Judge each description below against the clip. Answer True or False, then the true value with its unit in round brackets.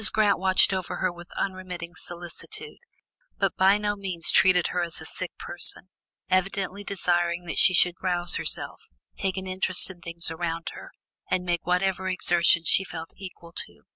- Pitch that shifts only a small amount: True (1.6 semitones)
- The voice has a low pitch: False (180 Hz)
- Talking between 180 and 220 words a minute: False (170 wpm)